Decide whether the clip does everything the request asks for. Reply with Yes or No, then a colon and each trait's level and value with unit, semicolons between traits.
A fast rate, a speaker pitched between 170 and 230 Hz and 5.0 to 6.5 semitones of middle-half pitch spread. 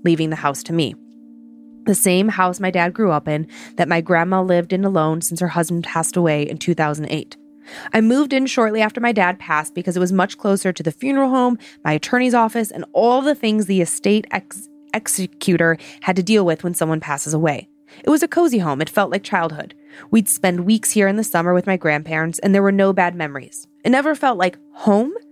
Yes: fast, 220 wpm; medium, 185 Hz; wide, 5.4 semitones